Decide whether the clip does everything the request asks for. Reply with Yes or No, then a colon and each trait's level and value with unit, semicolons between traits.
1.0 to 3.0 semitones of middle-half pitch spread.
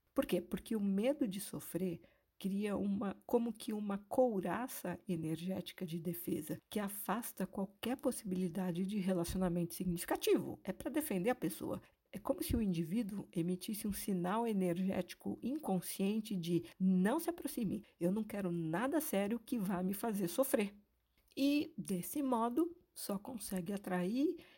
No: average, 5.0 semitones